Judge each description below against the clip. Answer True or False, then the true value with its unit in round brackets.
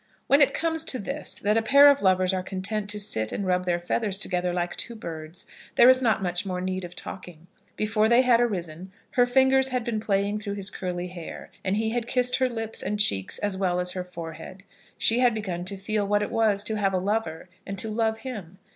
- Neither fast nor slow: False (230 wpm)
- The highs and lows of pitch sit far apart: False (3.8 semitones)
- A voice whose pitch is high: True (205 Hz)